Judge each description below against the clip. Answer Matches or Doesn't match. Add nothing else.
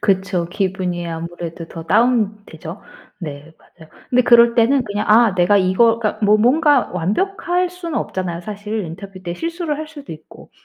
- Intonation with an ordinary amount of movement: Doesn't match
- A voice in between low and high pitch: Doesn't match